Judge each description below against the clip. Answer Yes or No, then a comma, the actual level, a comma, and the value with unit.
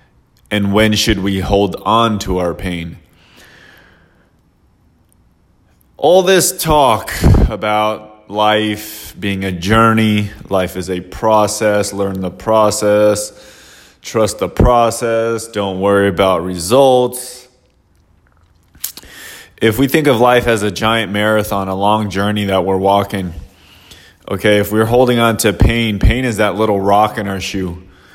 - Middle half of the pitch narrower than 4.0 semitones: Yes, average, 2.8 semitones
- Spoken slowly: Yes, slow, 130 wpm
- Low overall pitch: Yes, low, 105 Hz